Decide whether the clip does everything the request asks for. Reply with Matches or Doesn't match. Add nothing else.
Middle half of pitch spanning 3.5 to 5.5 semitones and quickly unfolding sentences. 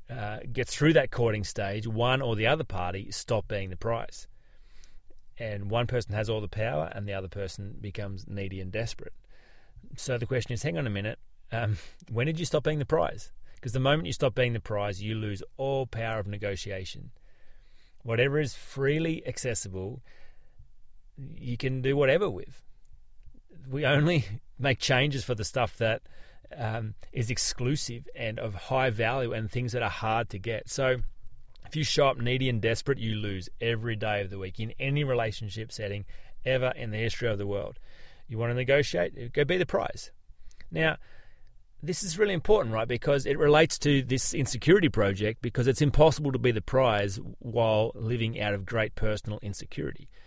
Doesn't match